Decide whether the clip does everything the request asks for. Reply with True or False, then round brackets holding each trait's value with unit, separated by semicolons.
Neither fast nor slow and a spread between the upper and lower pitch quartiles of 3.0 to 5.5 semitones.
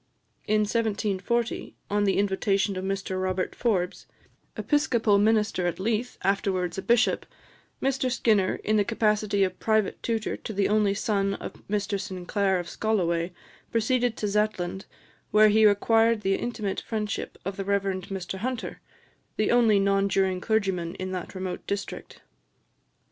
False (145 wpm; 2.4 semitones)